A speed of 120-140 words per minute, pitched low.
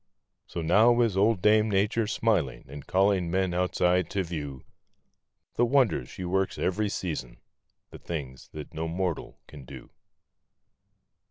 Yes: slow, 135 wpm; very low, 90 Hz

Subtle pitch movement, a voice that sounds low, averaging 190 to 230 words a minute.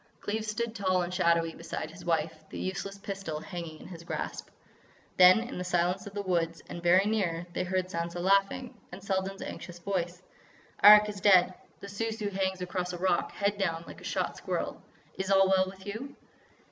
No: narrow, 2.3 semitones; high, 190 Hz; average, 195 wpm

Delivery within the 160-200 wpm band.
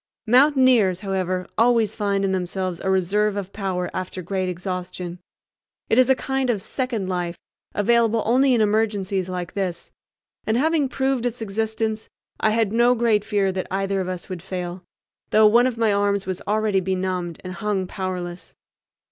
Yes: average, 165 wpm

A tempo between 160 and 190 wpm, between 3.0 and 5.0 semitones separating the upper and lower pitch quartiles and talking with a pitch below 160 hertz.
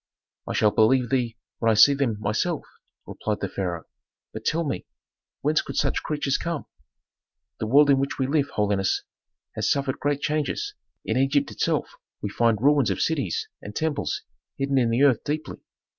Yes: average, 175 wpm; average, 4.7 semitones; low, 135 Hz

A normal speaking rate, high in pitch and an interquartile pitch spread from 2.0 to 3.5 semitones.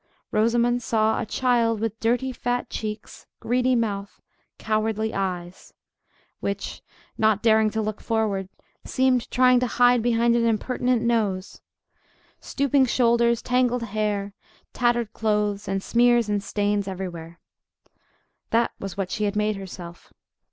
No: slow, 125 wpm; high, 220 Hz; average, 2.8 semitones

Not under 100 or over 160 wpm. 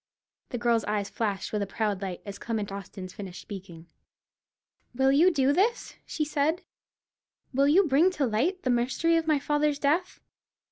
No: average, 170 wpm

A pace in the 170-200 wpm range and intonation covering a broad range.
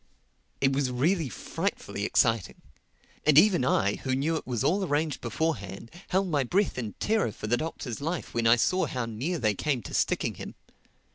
Yes: average, 185 wpm; wide, 5.9 semitones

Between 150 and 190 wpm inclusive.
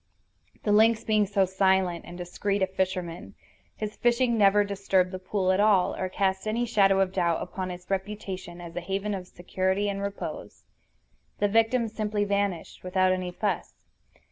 Yes: average, 170 wpm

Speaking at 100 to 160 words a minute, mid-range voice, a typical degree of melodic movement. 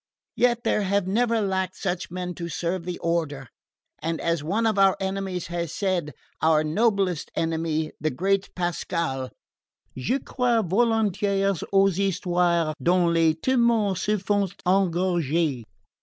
Yes: slow, 135 wpm; medium, 180 Hz; average, 3.0 semitones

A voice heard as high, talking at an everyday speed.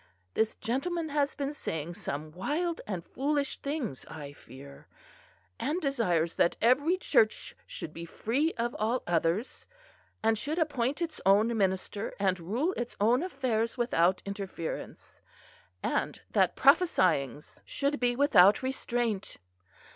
No: high, 230 Hz; slow, 130 wpm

